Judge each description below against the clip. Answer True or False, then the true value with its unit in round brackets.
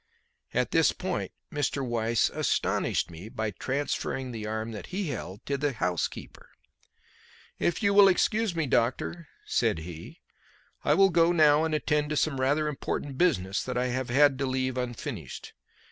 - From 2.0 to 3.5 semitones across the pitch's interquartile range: False (4.8 semitones)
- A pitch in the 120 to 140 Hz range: True (135 Hz)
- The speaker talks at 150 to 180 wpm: True (160 wpm)